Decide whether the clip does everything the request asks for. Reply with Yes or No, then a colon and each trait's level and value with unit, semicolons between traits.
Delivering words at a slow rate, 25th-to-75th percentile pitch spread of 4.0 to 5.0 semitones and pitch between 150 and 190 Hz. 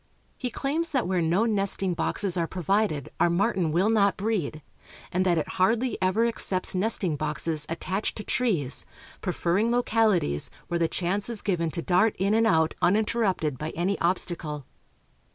No: average, 160 wpm; average, 4.5 semitones; medium, 185 Hz